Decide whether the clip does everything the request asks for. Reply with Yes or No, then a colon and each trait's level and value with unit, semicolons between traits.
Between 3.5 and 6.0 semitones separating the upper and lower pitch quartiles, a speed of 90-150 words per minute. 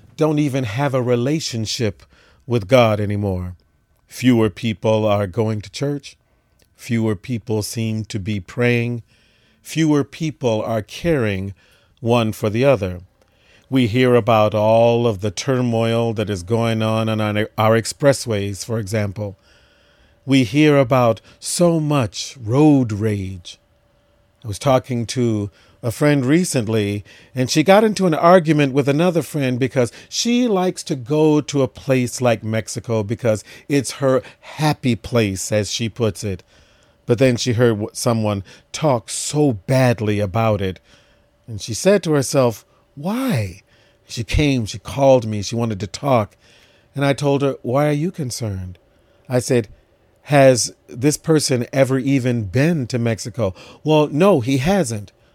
Yes: average, 4.2 semitones; average, 145 wpm